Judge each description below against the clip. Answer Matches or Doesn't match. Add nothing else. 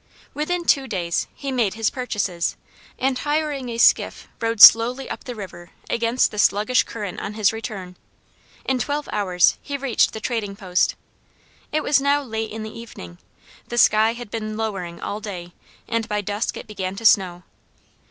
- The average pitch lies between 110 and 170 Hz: Doesn't match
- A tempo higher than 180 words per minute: Doesn't match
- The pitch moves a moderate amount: Matches